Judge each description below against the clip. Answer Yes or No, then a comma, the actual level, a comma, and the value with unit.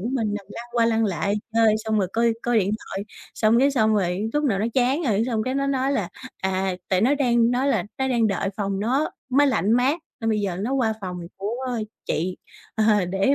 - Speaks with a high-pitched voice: Yes, high, 225 Hz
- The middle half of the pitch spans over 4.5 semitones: No, average, 4.2 semitones